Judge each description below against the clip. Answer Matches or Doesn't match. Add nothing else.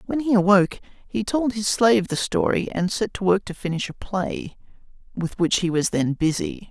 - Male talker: Matches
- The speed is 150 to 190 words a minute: Doesn't match